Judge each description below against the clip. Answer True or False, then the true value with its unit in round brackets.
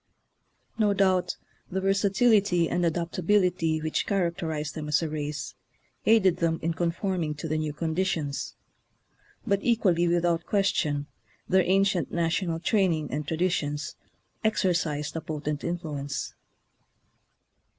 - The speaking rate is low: True (120 wpm)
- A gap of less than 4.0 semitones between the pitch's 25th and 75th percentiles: True (3.5 semitones)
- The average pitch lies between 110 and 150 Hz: False (170 Hz)